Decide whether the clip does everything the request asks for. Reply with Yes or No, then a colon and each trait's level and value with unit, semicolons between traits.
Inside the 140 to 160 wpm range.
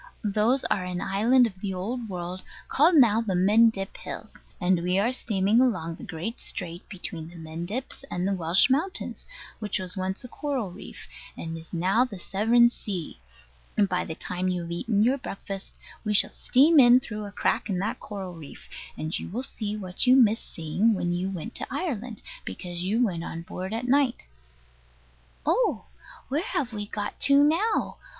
No: average, 185 wpm